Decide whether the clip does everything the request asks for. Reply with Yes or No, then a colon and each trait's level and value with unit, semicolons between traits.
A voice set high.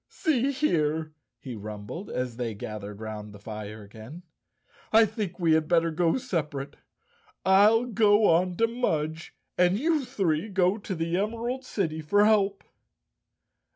No: medium, 175 Hz